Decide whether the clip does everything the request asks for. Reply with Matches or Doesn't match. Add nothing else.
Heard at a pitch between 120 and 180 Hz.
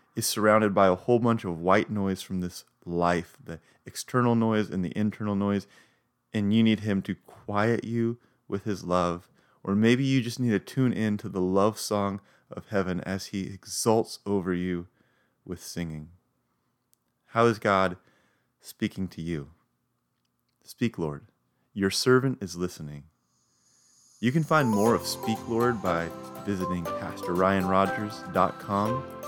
Doesn't match